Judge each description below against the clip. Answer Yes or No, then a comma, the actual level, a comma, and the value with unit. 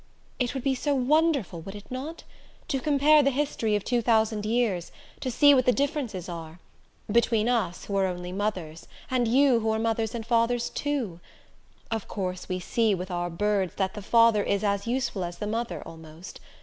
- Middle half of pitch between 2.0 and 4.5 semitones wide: No, average, 4.9 semitones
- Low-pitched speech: No, high, 220 Hz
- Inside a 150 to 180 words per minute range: No, average, 190 wpm